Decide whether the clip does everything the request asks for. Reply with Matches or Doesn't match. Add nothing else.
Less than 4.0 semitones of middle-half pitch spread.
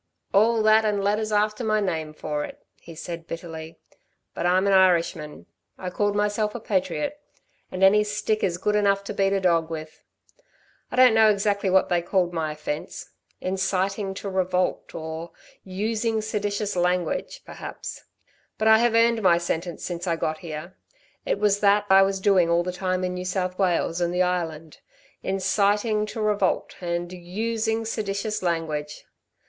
Matches